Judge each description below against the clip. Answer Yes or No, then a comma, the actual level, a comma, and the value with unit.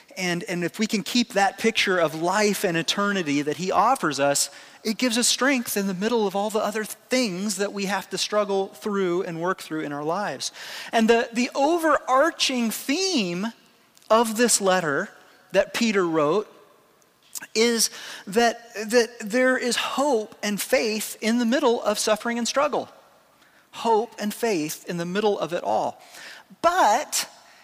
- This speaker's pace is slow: No, average, 165 wpm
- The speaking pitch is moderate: No, high, 215 Hz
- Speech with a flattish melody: No, average, 3.8 semitones